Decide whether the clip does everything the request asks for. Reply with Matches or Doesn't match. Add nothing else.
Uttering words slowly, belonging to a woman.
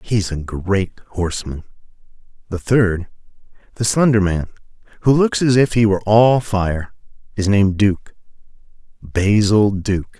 Doesn't match